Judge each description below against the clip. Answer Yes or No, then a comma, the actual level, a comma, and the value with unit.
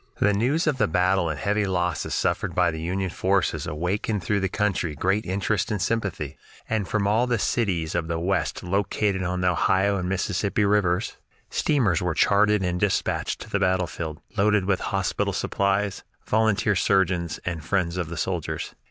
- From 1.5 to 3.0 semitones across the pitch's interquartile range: Yes, average, 2.7 semitones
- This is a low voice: Yes, very low, 95 Hz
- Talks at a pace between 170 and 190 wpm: Yes, average, 180 wpm